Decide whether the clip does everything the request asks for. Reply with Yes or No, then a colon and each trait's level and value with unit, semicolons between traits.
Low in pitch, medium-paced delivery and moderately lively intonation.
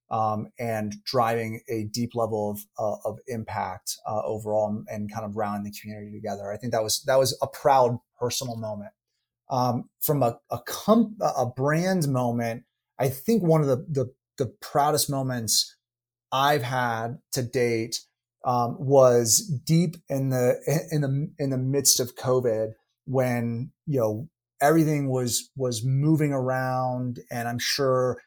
Yes: low, 125 Hz; average, 155 wpm; average, 3.0 semitones